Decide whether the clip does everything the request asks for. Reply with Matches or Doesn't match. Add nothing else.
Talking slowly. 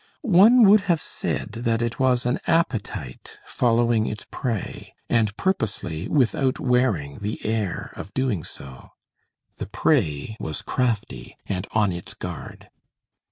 Matches